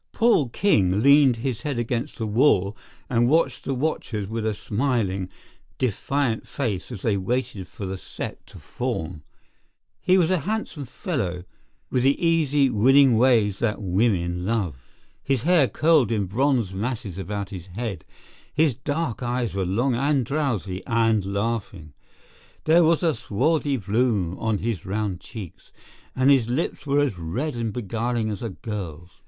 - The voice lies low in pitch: Yes, low, 115 Hz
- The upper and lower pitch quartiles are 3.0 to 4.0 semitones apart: No, wide, 5.6 semitones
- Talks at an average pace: Yes, average, 155 wpm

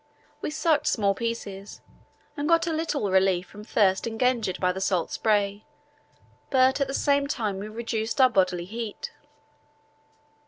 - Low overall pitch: No, high, 220 Hz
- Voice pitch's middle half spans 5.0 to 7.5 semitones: Yes, wide, 5.4 semitones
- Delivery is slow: No, average, 150 wpm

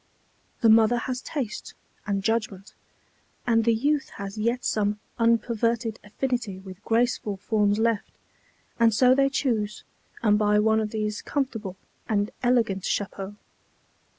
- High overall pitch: Yes, high, 220 Hz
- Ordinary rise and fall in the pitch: No, narrow, 2.3 semitones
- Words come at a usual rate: No, slow, 130 wpm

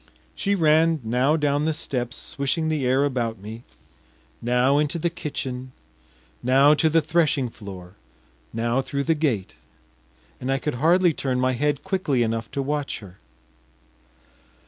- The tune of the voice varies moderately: Yes, average, 4.0 semitones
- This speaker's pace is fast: No, average, 145 wpm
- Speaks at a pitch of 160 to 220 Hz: No, medium, 140 Hz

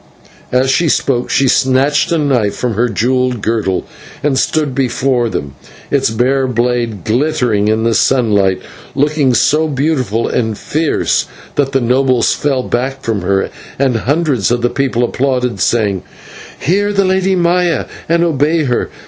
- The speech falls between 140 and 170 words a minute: Yes, average, 150 wpm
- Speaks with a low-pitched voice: Yes, low, 130 Hz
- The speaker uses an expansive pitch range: No, average, 3.8 semitones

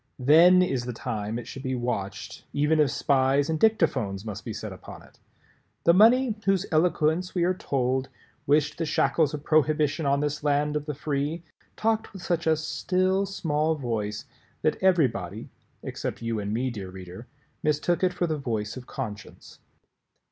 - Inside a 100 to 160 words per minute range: No, average, 170 wpm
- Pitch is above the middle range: No, medium, 150 Hz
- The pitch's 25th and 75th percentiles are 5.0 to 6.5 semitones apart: Yes, wide, 5.4 semitones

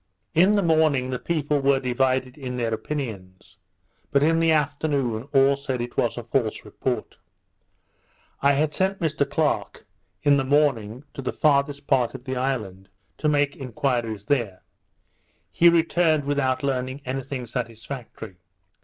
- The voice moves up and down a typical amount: Yes, average, 3.0 semitones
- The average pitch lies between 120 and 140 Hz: Yes, low, 135 Hz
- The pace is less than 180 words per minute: Yes, average, 150 wpm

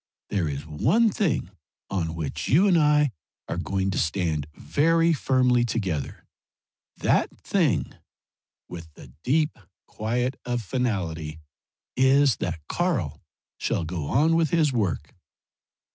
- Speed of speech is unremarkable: No, slow, 125 wpm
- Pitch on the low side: Yes, low, 115 Hz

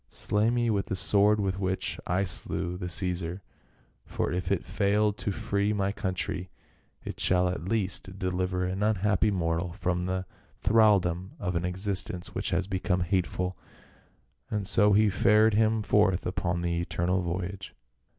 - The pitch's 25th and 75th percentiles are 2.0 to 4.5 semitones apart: Yes, narrow, 2.4 semitones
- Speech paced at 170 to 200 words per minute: No, average, 160 wpm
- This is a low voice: Yes, very low, 95 Hz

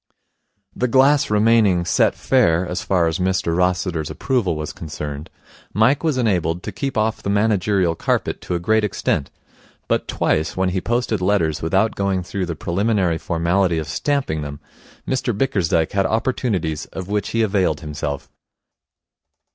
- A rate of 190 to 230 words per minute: No, average, 155 wpm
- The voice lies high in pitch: No, very low, 95 Hz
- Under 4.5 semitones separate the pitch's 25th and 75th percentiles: No, average, 4.8 semitones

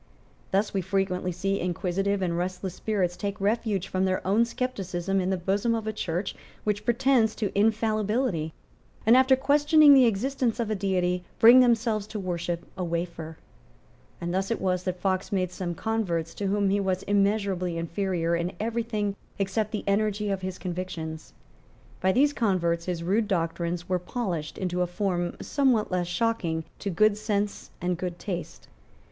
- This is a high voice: Yes, high, 195 Hz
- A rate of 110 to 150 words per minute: No, average, 170 wpm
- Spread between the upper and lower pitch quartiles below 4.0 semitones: Yes, average, 3.4 semitones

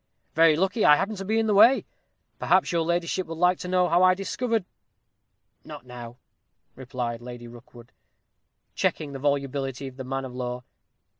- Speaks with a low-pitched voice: No, medium, 150 Hz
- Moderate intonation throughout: No, wide, 6.5 semitones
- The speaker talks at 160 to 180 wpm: Yes, average, 175 wpm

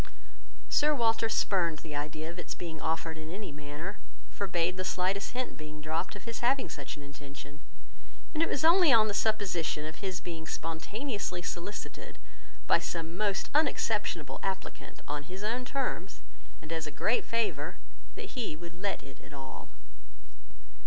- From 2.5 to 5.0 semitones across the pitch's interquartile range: No, wide, 5.4 semitones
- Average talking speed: Yes, average, 165 wpm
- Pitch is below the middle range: No, medium, 180 Hz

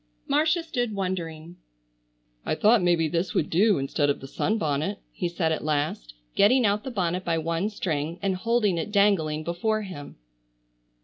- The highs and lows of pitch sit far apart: No, average, 4.7 semitones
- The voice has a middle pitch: Yes, medium, 180 Hz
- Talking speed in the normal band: Yes, average, 165 wpm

